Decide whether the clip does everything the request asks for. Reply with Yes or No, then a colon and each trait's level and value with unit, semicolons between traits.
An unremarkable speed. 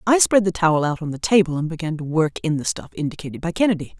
No: fast, 270 wpm